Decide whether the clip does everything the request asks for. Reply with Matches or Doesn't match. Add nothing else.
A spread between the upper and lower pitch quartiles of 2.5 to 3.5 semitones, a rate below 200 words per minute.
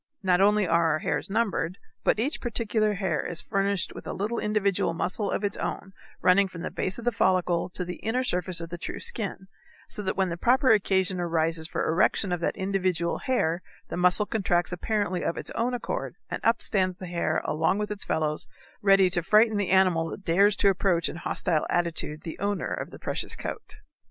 Doesn't match